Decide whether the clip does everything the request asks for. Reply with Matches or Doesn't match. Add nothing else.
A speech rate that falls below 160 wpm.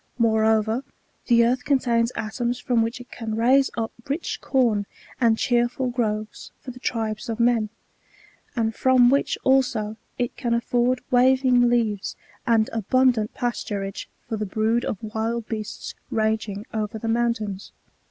Matches